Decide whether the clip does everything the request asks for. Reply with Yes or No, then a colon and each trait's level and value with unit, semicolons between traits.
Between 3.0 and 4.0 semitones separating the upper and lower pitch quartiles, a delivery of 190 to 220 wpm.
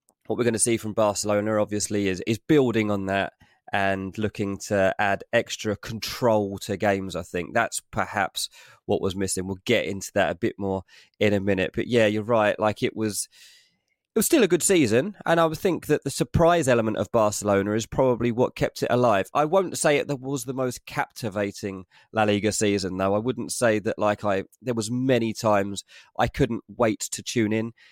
Yes: average, 3.6 semitones; fast, 205 wpm